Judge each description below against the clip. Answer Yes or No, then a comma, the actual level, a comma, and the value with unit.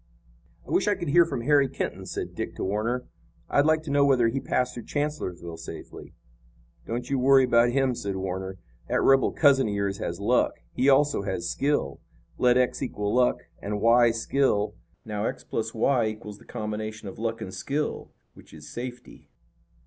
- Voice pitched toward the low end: Yes, low, 120 Hz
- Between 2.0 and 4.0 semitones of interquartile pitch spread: No, average, 4.8 semitones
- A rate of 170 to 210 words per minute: Yes, average, 185 wpm